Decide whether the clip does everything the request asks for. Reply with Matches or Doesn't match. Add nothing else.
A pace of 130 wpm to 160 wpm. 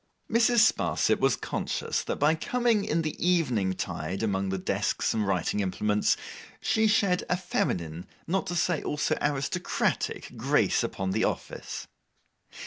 Matches